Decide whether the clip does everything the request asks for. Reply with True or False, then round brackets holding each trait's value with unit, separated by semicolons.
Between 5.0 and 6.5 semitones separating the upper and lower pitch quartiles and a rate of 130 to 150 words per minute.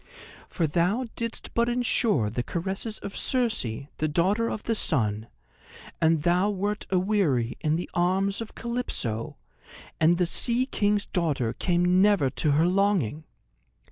True (5.4 semitones; 140 wpm)